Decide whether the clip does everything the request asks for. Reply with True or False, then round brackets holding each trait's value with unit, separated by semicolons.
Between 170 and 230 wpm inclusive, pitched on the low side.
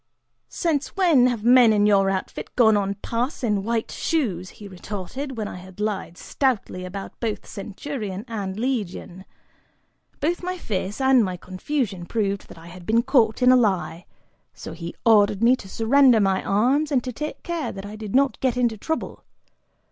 False (180 wpm; 220 Hz)